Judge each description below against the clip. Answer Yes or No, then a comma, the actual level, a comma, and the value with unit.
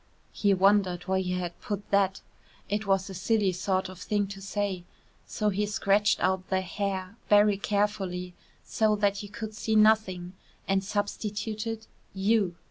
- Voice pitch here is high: Yes, high, 200 Hz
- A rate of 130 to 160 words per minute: Yes, average, 155 wpm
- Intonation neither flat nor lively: No, narrow, 1.8 semitones